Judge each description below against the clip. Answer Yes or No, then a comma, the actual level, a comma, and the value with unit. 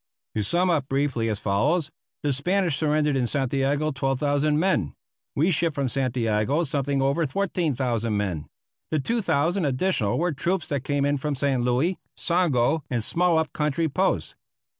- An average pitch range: Yes, average, 3.9 semitones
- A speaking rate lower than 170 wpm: Yes, average, 155 wpm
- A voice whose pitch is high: No, medium, 145 Hz